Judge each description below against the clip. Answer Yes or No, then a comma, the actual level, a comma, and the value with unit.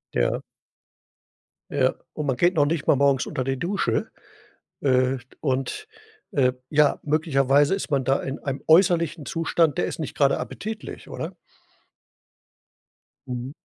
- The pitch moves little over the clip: No, average, 3.5 semitones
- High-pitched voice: No, medium, 145 Hz